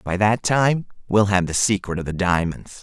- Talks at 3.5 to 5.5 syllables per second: Yes, 4.7 syllables/s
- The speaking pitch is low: Yes, low, 100 Hz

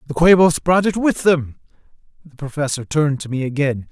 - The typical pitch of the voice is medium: Yes, medium, 150 Hz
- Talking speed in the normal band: Yes, average, 185 wpm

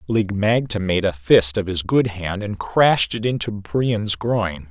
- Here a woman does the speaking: No, male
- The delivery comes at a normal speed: Yes, average, 190 wpm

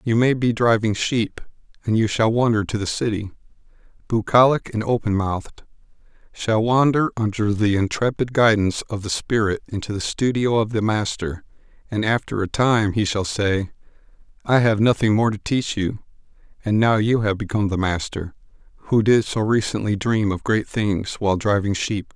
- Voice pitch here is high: No, low, 110 Hz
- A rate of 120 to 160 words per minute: No, average, 170 wpm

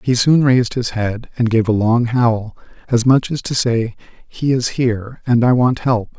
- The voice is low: Yes, low, 120 Hz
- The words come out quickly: Yes, fast, 215 wpm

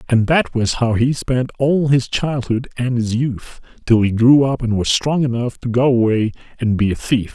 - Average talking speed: No, fast, 220 wpm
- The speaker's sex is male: Yes, male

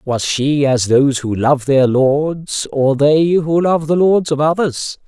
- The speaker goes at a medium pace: Yes, average, 190 wpm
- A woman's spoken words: No, male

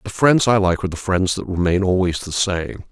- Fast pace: Yes, fast, 245 wpm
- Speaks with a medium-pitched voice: No, very low, 95 Hz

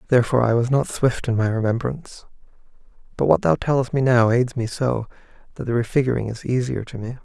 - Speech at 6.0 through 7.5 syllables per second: Yes, 6.3 syllables/s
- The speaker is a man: Yes, male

